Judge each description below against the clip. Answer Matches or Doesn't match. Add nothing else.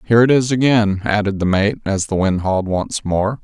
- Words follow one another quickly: Matches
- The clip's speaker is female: Doesn't match